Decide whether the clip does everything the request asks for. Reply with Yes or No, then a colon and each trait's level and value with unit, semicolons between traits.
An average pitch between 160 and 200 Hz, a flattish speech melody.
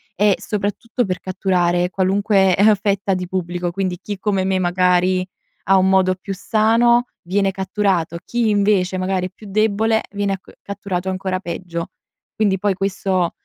Yes: high, 190 Hz; narrow, 1.9 semitones